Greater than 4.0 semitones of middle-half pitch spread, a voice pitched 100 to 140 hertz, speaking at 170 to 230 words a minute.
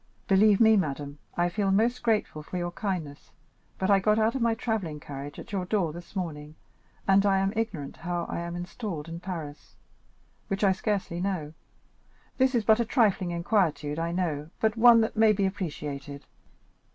No: average, 5.0 semitones; medium, 185 Hz; average, 180 wpm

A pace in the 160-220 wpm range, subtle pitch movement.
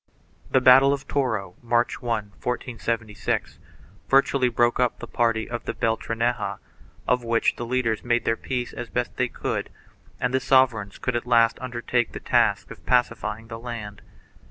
Yes: average, 165 wpm; narrow, 1.7 semitones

